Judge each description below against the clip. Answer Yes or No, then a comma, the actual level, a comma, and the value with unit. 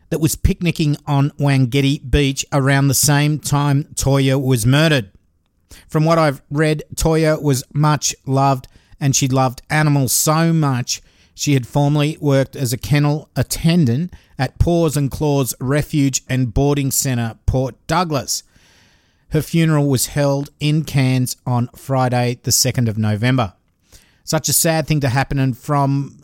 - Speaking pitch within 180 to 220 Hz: No, medium, 140 Hz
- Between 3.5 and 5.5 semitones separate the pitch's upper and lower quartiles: No, average, 2.8 semitones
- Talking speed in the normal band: Yes, average, 150 wpm